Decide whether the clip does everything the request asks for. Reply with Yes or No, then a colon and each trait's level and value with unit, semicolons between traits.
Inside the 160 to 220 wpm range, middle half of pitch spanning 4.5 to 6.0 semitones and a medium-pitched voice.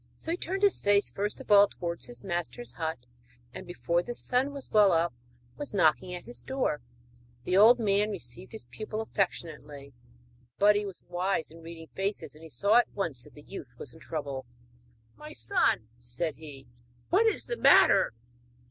Yes: average, 180 wpm; wide, 5.5 semitones; medium, 180 Hz